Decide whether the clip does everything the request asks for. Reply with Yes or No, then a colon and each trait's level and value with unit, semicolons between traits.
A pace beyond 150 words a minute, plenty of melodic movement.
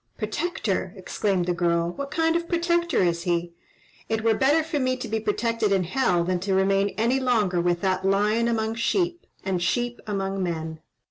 Yes: average, 190 wpm; wide, 5.8 semitones